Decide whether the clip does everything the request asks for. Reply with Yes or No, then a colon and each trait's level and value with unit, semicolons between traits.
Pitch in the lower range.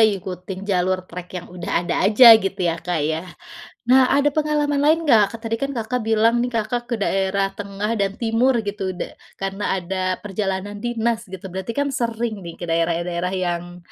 No: high, 200 Hz